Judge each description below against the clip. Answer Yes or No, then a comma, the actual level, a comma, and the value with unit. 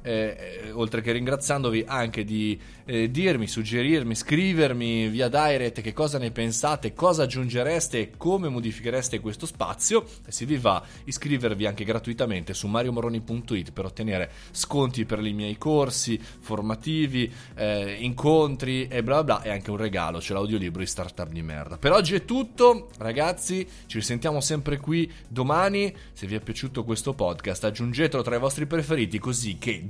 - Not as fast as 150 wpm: No, average, 165 wpm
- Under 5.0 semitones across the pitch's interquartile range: No, average, 5.3 semitones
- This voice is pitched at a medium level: No, low, 120 Hz